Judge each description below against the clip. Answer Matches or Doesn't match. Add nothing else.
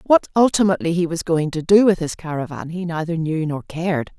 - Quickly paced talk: Matches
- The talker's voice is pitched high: Doesn't match